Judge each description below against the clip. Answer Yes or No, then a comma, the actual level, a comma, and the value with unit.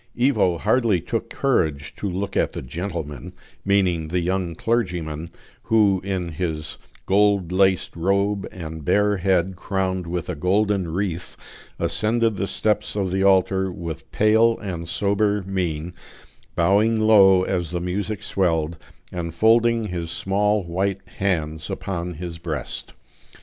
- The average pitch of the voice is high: No, very low, 95 Hz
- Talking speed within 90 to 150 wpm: Yes, slow, 135 wpm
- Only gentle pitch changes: No, average, 3.1 semitones